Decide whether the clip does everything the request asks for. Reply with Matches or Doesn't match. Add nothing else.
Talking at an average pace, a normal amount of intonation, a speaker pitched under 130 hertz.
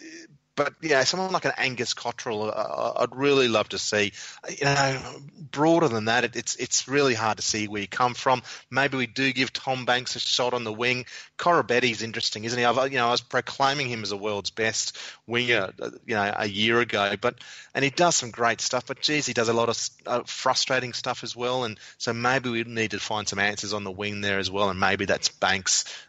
Doesn't match